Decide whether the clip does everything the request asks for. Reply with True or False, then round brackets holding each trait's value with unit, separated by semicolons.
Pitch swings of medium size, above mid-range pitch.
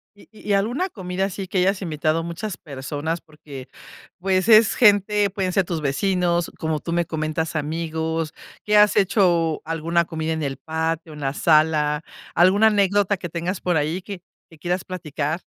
False (3.5 semitones; 170 Hz)